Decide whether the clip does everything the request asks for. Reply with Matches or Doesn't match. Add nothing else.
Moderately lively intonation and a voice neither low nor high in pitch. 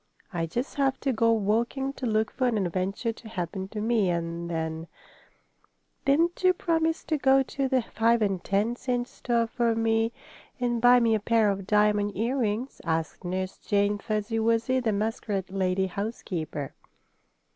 Doesn't match